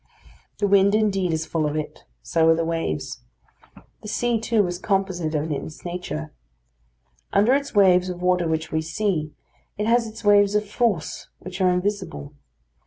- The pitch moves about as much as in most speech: Yes, average, 4.2 semitones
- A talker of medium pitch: Yes, medium, 180 Hz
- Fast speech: No, average, 170 wpm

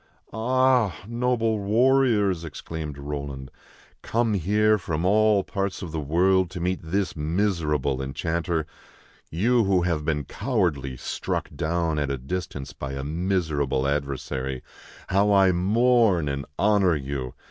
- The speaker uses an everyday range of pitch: No, wide, 6.0 semitones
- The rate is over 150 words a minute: No, average, 140 wpm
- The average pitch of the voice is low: Yes, very low, 85 Hz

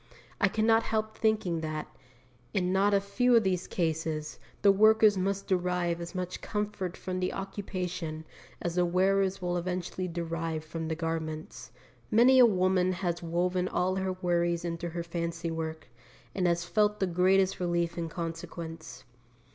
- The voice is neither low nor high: Yes, medium, 180 Hz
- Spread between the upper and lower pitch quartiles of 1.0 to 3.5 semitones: Yes, narrow, 2.5 semitones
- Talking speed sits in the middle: Yes, average, 160 wpm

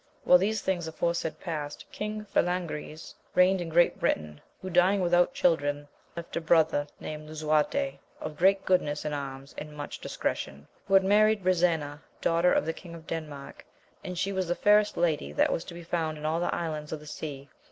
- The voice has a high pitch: No, medium, 165 Hz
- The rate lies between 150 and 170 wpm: No, average, 190 wpm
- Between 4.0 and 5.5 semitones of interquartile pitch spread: No, average, 3.2 semitones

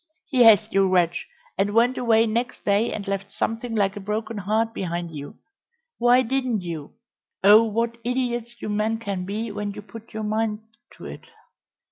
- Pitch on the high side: Yes, high, 215 Hz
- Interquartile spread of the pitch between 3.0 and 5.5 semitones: No, narrow, 2.6 semitones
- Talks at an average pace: Yes, average, 170 wpm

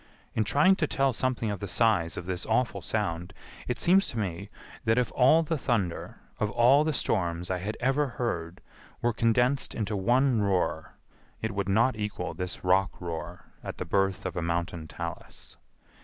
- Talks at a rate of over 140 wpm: Yes, average, 180 wpm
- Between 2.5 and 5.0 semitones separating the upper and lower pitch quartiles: No, wide, 5.6 semitones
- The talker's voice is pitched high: No, low, 105 Hz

